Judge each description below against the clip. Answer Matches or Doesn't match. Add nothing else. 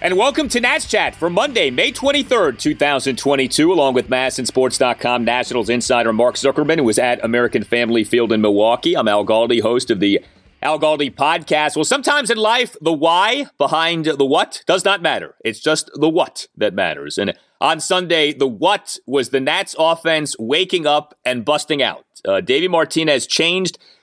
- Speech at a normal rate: Matches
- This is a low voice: Doesn't match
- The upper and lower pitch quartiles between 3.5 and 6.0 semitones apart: Matches